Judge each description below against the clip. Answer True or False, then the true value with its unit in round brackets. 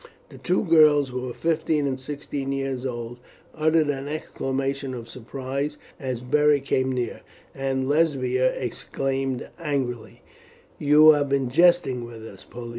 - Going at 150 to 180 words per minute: False (140 wpm)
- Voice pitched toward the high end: False (135 Hz)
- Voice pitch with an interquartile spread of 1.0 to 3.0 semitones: True (2.6 semitones)